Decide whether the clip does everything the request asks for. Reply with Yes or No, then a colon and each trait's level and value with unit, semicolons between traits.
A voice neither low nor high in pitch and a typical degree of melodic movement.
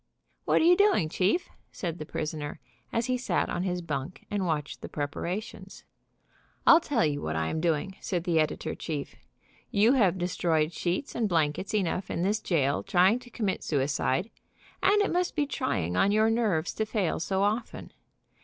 No: medium, 180 Hz; wide, 5.7 semitones